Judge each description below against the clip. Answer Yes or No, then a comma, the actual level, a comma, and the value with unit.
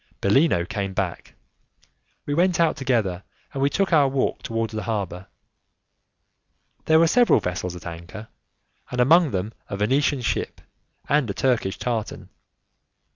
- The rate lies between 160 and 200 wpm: No, average, 140 wpm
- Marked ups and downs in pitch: Yes, wide, 6.7 semitones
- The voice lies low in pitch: Yes, low, 115 Hz